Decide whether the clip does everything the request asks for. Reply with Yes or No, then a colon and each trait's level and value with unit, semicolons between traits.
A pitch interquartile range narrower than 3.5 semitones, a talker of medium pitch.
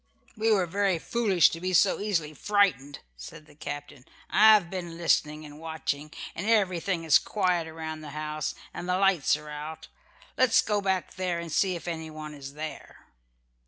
No: average, 3.9 semitones; medium, 165 Hz